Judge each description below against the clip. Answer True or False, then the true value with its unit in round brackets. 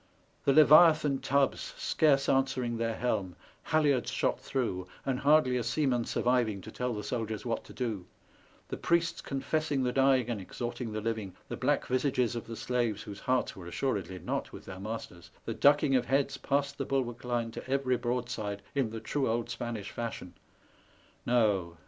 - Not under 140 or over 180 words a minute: True (175 wpm)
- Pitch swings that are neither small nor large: True (3.6 semitones)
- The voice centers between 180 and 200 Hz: False (125 Hz)